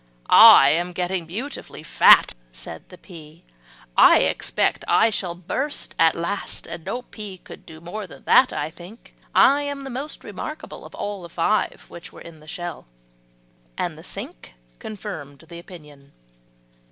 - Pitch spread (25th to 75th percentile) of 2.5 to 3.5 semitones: No, average, 4.9 semitones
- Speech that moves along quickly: No, average, 155 wpm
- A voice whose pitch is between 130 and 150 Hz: No, medium, 175 Hz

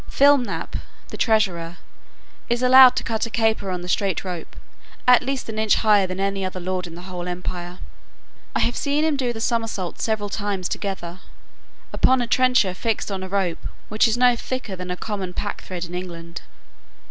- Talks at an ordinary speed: Yes, average, 185 wpm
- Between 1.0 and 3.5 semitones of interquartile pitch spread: No, average, 4.5 semitones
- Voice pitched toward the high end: Yes, high, 200 Hz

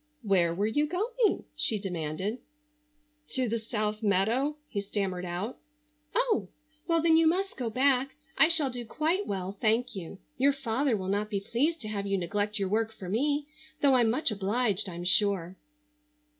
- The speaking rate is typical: Yes, average, 170 wpm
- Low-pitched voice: No, high, 220 Hz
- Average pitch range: No, wide, 6.0 semitones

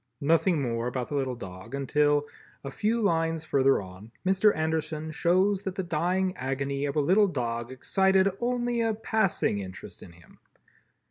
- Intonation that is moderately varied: No, wide, 6.5 semitones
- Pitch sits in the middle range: Yes, medium, 155 Hz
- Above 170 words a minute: No, average, 160 wpm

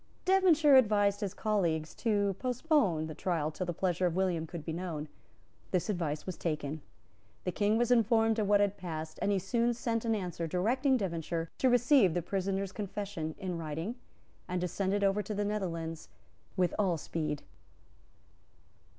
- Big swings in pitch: No, average, 4.4 semitones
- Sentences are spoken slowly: No, average, 170 wpm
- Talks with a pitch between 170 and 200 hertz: Yes, high, 190 Hz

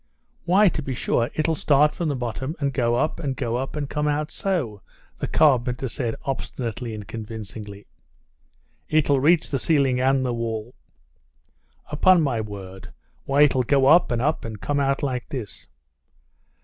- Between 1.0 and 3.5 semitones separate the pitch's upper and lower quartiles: No, average, 4.2 semitones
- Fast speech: No, average, 165 wpm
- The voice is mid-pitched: No, low, 130 Hz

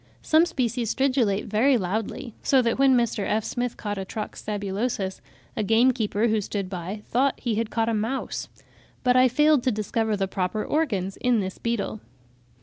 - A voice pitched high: Yes, high, 225 Hz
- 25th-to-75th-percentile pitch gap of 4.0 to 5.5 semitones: No, average, 3.4 semitones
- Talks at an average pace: Yes, average, 175 wpm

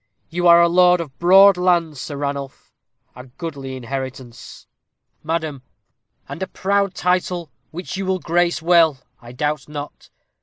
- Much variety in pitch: No, average, 4.2 semitones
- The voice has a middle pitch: Yes, medium, 165 Hz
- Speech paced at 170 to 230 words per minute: No, average, 140 wpm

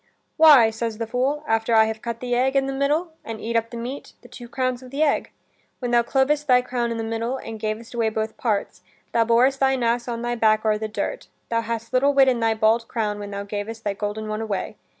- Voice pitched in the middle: No, high, 235 Hz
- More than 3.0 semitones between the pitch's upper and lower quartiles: No, average, 2.7 semitones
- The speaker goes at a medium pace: No, fast, 250 wpm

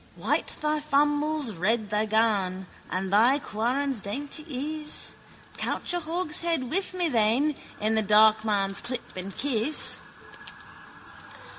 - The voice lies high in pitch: Yes, high, 245 Hz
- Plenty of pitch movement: Yes, wide, 6.1 semitones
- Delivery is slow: Yes, slow, 120 wpm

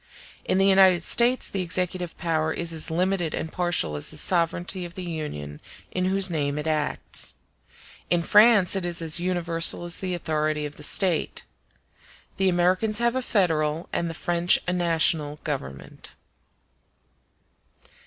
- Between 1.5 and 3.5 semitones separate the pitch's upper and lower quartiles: Yes, average, 2.8 semitones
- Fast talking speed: No, average, 155 wpm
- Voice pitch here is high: No, medium, 175 Hz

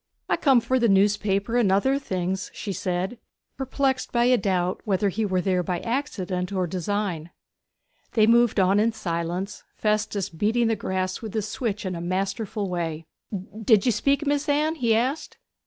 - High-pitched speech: Yes, high, 205 Hz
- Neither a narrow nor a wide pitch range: Yes, average, 4.2 semitones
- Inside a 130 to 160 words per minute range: No, average, 170 wpm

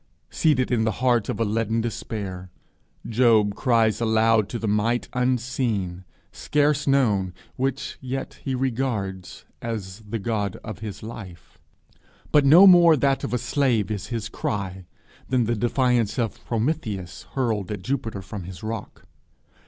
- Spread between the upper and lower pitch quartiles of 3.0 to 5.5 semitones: Yes, average, 3.8 semitones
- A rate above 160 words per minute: No, average, 145 wpm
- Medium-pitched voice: No, low, 115 Hz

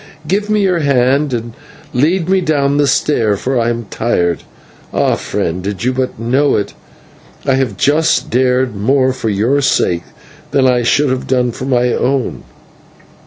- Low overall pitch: Yes, low, 130 Hz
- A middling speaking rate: Yes, average, 165 wpm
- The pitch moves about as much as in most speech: Yes, average, 3.4 semitones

